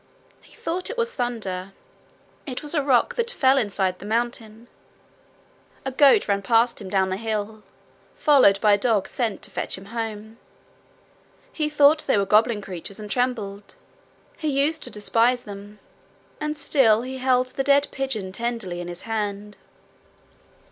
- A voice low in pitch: No, high, 230 Hz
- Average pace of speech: Yes, average, 160 wpm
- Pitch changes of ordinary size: Yes, average, 4.8 semitones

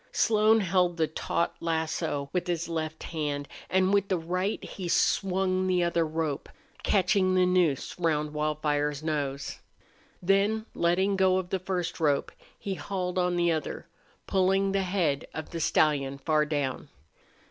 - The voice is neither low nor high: Yes, medium, 175 Hz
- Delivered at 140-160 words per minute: Yes, average, 150 wpm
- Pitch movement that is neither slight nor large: Yes, average, 3.4 semitones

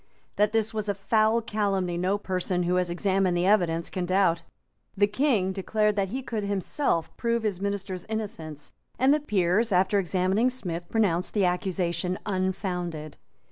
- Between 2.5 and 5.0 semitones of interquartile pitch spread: Yes, average, 3.0 semitones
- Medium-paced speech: Yes, average, 160 wpm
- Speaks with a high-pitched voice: Yes, high, 195 Hz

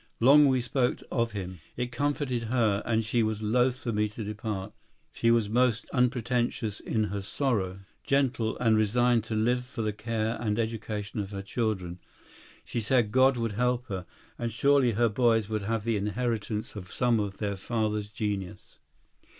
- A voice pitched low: Yes, low, 115 Hz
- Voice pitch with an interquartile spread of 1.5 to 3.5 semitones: Yes, average, 2.7 semitones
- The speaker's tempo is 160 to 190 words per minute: Yes, average, 175 wpm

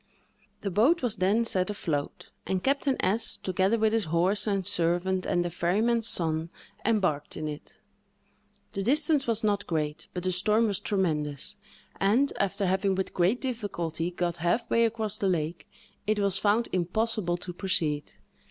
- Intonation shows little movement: No, average, 4.0 semitones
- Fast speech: No, average, 160 wpm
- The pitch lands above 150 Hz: Yes, high, 190 Hz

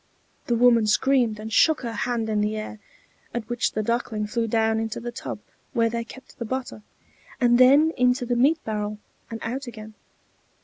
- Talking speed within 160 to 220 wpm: Yes, average, 185 wpm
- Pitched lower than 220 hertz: No, high, 235 Hz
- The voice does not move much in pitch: Yes, narrow, 2.3 semitones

